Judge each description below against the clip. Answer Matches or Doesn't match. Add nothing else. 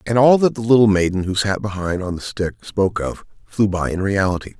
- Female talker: Doesn't match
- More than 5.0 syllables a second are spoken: Matches